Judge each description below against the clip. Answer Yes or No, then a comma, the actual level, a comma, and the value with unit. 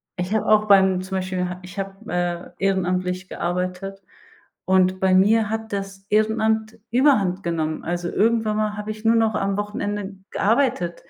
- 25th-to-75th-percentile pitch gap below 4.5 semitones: Yes, average, 2.8 semitones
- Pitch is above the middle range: Yes, high, 195 Hz